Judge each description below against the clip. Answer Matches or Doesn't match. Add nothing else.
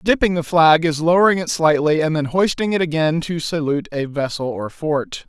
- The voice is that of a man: Matches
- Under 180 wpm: Doesn't match